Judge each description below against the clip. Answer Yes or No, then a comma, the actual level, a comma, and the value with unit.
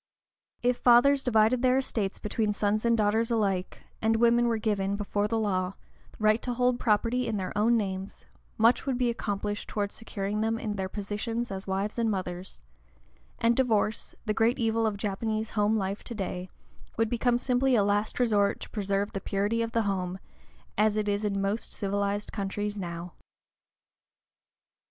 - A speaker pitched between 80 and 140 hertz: No, high, 215 Hz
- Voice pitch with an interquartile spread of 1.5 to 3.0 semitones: Yes, narrow, 2.5 semitones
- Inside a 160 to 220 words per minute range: Yes, average, 170 wpm